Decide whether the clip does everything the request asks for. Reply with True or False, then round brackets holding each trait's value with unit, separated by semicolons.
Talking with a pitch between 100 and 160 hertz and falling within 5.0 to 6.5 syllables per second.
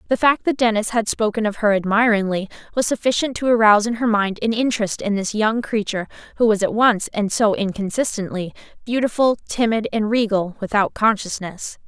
False (215 Hz; 5.6 syllables/s)